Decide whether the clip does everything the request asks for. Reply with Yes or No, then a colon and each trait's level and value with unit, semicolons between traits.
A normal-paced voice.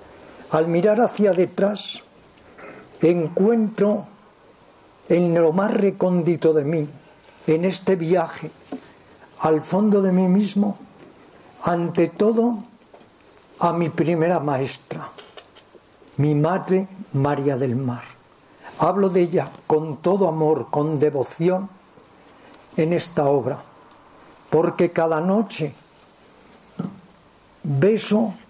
No: slow, 95 wpm